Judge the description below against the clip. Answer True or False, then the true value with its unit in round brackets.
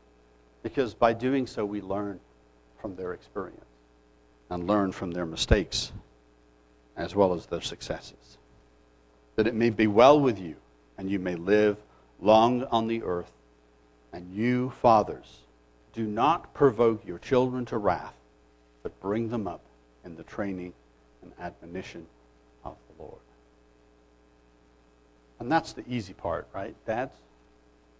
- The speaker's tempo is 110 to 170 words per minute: True (135 wpm)